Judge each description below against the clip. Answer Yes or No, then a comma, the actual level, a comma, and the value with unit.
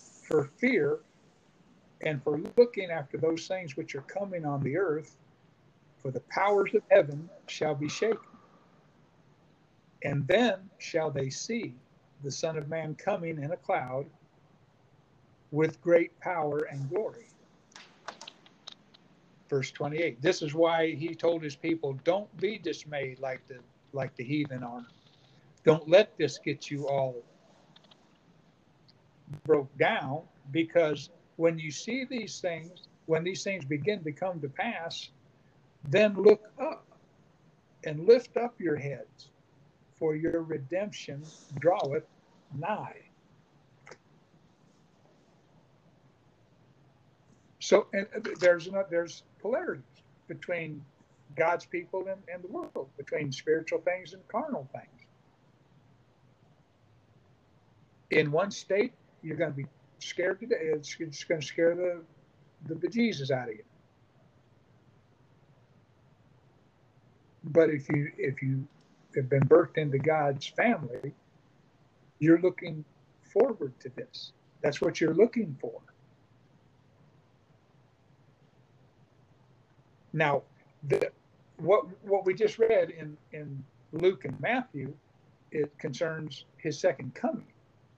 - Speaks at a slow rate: Yes, slow, 115 wpm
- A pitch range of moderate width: Yes, average, 3.8 semitones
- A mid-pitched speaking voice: Yes, medium, 150 Hz